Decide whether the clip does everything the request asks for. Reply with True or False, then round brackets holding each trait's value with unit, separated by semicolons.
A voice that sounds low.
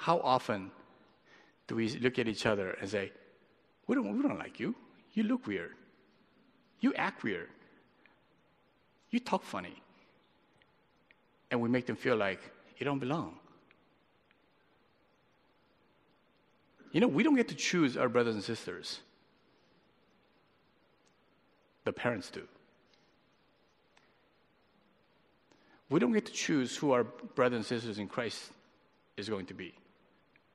True (125 Hz)